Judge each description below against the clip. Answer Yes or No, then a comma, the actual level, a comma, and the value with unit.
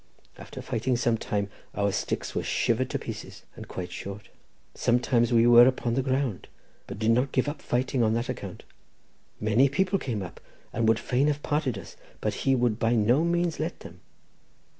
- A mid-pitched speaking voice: No, low, 120 Hz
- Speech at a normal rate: Yes, average, 190 wpm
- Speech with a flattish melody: No, average, 3.2 semitones